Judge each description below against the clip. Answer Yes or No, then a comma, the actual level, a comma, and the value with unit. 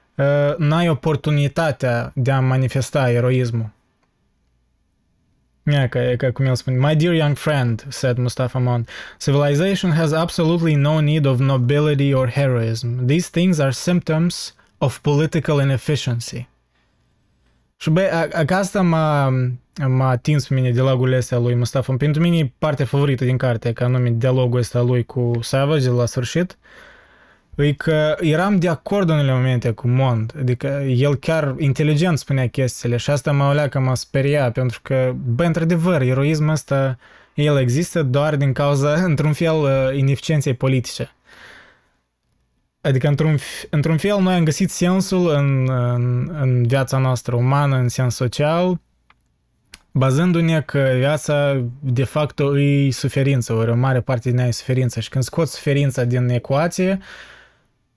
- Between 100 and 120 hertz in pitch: No, low, 135 Hz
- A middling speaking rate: Yes, average, 145 wpm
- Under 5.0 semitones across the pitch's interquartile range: Yes, average, 3.4 semitones